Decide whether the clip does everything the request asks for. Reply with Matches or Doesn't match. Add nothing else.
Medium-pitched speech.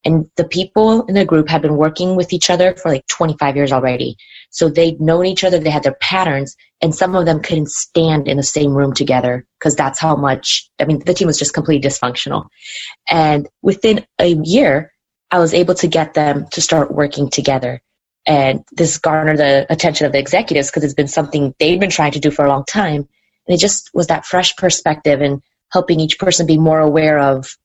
Matches